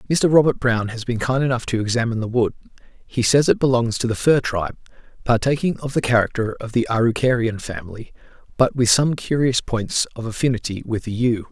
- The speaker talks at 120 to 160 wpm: No, average, 195 wpm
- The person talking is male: Yes, male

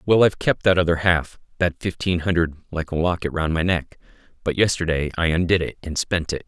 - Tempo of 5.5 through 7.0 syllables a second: Yes, 5.7 syllables/s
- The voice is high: No, very low, 85 Hz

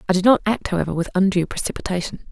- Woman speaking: Yes, female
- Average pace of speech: No, fast, 210 wpm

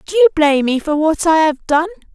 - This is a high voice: Yes, very high, 320 Hz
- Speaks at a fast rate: Yes, fast, 250 wpm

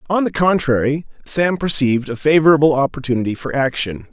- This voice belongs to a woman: No, male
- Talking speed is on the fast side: No, average, 145 wpm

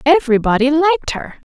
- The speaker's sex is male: No, female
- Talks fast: No, slow, 115 wpm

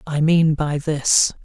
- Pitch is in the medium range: Yes, medium, 150 Hz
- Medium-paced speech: Yes, average, 165 wpm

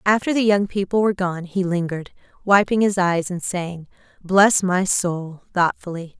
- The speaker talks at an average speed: Yes, average, 165 wpm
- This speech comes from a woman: Yes, female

